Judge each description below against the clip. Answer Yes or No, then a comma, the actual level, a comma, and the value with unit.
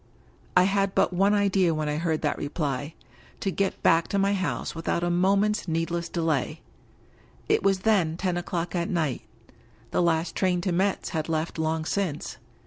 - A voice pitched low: No, medium, 175 Hz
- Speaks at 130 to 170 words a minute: No, average, 185 wpm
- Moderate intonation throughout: Yes, average, 3.2 semitones